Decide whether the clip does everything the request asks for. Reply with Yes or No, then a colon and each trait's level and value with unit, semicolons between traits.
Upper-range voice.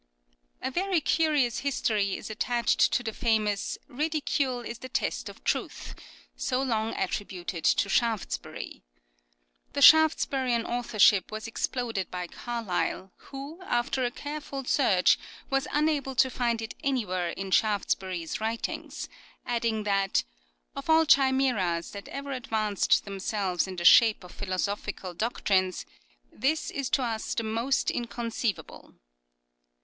Yes: high, 230 Hz